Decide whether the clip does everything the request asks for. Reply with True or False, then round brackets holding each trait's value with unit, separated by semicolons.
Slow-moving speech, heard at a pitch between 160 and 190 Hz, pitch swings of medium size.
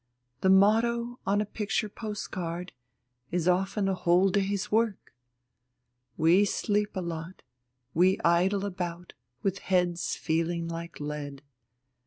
True (120 wpm; 185 Hz; 3.1 semitones)